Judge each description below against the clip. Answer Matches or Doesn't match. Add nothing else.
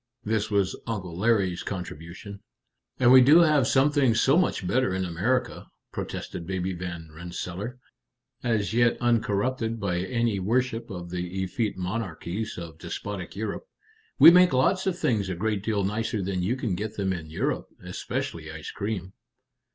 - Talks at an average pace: Matches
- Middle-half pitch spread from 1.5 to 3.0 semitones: Doesn't match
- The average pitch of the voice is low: Matches